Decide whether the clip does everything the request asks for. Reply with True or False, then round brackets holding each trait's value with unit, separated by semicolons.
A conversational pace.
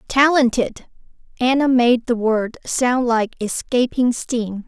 False (115 wpm)